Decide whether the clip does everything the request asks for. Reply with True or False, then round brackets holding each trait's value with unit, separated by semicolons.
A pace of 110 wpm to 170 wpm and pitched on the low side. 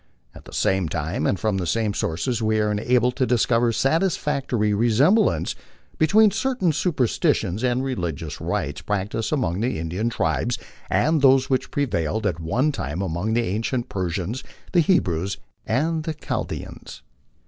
True (150 wpm; 115 Hz)